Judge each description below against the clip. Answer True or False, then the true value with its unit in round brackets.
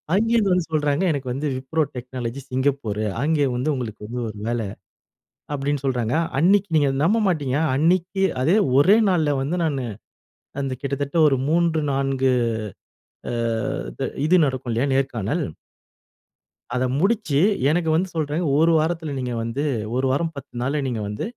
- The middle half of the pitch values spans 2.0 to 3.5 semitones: False (4.0 semitones)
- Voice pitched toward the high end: False (145 Hz)